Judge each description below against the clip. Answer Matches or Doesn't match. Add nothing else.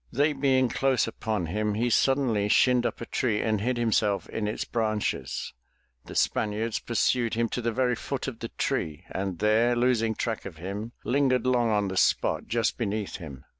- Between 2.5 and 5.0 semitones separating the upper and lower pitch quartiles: Matches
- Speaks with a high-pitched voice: Doesn't match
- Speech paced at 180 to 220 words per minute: Matches